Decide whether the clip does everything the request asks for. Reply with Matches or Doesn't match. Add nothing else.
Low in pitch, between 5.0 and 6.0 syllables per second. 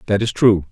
Matches